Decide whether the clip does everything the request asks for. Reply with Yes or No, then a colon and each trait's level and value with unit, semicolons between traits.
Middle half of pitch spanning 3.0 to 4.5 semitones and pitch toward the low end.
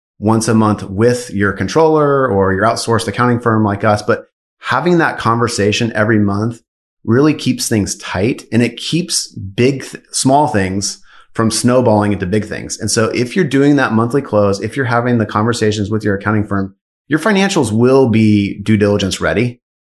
Yes: average, 3.4 semitones; low, 110 Hz